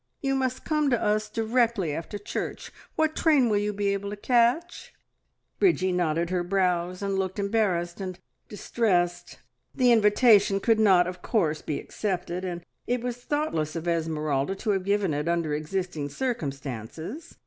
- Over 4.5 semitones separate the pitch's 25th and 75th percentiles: Yes, average, 4.9 semitones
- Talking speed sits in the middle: Yes, average, 160 wpm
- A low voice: No, high, 195 Hz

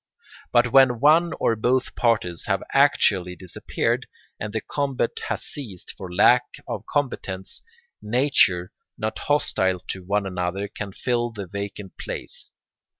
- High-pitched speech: No, low, 105 Hz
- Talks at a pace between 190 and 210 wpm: No, slow, 135 wpm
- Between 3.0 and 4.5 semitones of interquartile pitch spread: No, average, 4.9 semitones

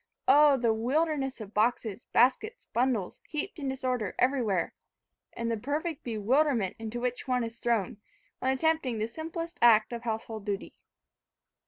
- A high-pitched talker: Yes, high, 245 Hz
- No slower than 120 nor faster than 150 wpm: Yes, average, 145 wpm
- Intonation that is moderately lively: Yes, average, 4.0 semitones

